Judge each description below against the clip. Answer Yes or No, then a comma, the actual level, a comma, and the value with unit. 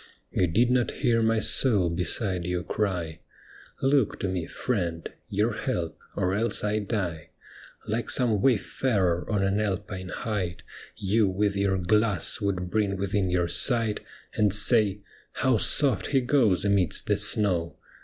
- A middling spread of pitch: Yes, average, 3.5 semitones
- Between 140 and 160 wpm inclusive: Yes, average, 155 wpm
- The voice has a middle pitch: No, low, 100 Hz